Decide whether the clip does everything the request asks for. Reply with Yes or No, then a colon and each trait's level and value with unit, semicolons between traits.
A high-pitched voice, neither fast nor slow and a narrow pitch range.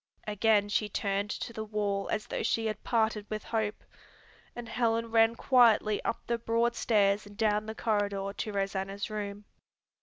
Yes: high, 215 Hz; average, 170 wpm; narrow, 1.7 semitones